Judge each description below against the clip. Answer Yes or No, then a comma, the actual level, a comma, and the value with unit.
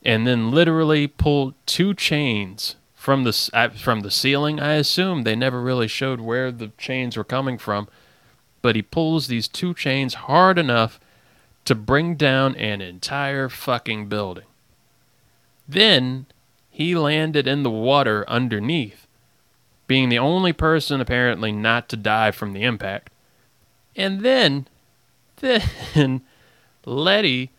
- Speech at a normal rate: No, slow, 130 wpm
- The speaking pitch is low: Yes, low, 130 Hz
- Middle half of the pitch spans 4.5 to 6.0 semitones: No, average, 4.1 semitones